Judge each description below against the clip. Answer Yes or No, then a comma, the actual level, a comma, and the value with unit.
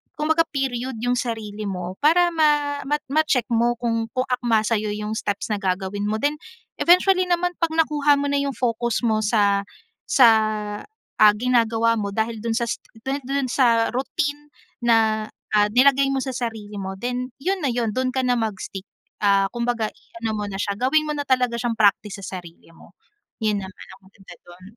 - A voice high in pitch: Yes, high, 235 Hz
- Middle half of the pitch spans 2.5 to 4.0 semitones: No, average, 4.6 semitones